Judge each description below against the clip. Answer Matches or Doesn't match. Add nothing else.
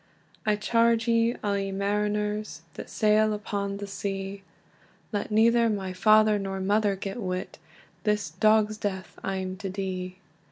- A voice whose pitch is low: Doesn't match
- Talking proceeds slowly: Doesn't match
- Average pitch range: Doesn't match